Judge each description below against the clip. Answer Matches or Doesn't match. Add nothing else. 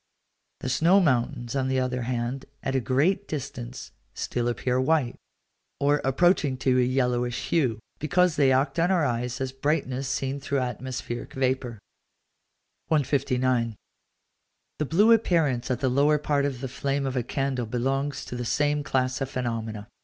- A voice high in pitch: Doesn't match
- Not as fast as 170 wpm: Matches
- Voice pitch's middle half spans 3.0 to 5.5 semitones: Doesn't match